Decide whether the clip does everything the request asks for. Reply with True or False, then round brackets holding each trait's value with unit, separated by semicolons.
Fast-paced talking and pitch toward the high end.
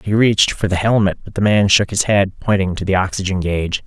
False (250 wpm; 95 Hz)